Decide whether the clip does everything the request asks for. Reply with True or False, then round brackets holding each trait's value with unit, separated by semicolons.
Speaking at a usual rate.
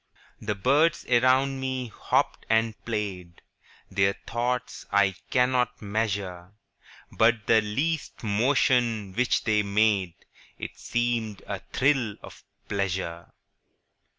False (105 wpm)